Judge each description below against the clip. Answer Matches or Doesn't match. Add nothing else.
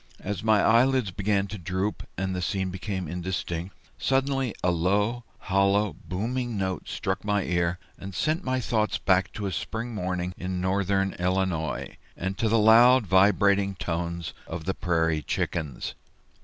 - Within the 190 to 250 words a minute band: Doesn't match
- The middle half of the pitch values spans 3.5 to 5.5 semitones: Doesn't match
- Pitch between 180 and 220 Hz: Doesn't match